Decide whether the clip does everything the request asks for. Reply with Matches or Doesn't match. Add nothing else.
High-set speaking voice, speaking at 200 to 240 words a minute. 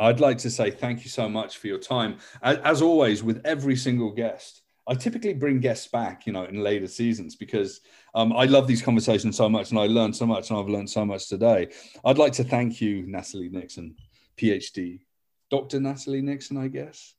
Doesn't match